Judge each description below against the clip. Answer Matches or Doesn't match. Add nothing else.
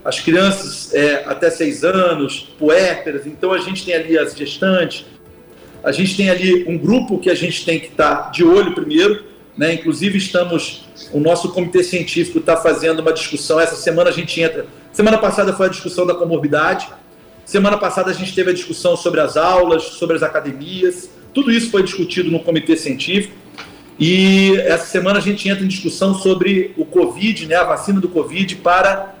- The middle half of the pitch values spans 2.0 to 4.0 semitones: Matches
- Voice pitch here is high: Doesn't match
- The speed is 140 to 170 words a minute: Doesn't match